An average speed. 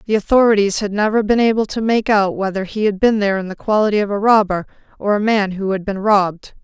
No: fast, 245 wpm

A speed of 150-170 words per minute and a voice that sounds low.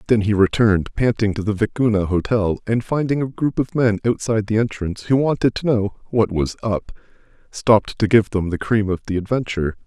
No: average, 200 wpm; low, 110 Hz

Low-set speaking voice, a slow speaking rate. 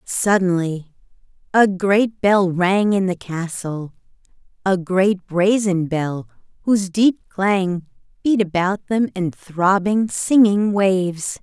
No: high, 190 Hz; slow, 115 wpm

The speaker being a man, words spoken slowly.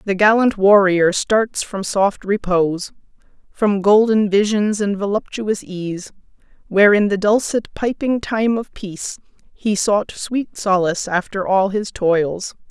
No: female; slow, 130 wpm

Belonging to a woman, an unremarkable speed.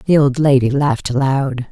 Yes: female; average, 175 wpm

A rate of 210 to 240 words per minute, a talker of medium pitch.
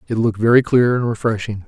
No: fast, 215 wpm; low, 115 Hz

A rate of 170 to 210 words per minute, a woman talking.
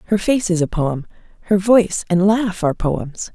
Yes: average, 200 wpm; female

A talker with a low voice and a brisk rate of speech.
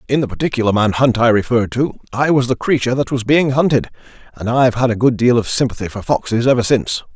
Yes: low, 120 Hz; fast, 235 wpm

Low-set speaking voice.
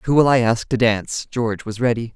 Yes: low, 115 Hz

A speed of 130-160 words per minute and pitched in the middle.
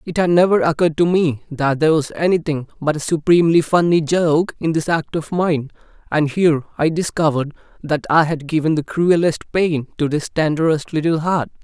No: average, 185 wpm; medium, 160 Hz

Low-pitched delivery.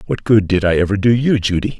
Yes: low, 105 Hz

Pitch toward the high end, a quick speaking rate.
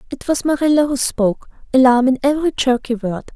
No: very high, 260 Hz; average, 180 wpm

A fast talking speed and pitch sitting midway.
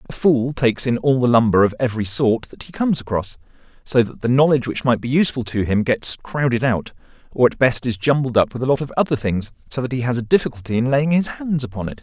No: fast, 255 wpm; low, 125 Hz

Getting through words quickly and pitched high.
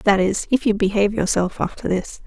Yes: fast, 210 wpm; high, 205 Hz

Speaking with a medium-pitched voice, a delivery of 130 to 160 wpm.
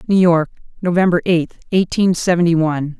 Yes: medium, 170 Hz; average, 140 wpm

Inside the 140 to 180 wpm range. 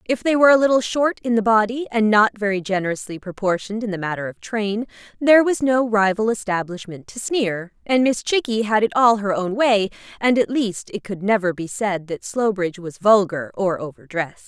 No: fast, 205 wpm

